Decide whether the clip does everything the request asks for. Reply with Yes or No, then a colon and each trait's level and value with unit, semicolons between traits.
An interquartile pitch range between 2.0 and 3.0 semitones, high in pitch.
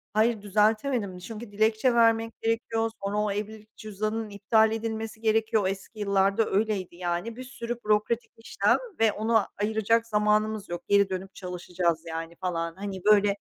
Yes: narrow, 2.4 semitones; high, 215 Hz